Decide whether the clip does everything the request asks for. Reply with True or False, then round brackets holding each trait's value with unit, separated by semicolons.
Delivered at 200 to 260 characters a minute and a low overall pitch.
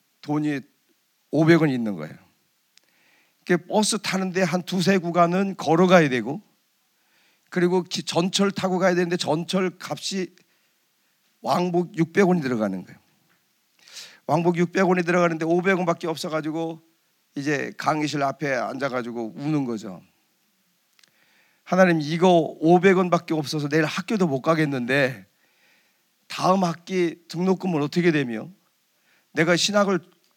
False (255 characters per minute; 170 Hz)